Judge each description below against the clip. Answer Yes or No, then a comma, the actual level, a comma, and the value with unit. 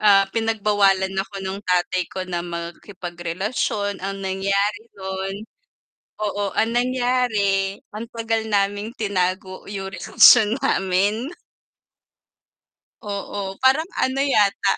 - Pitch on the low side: No, high, 200 Hz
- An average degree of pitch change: No, narrow, 2.3 semitones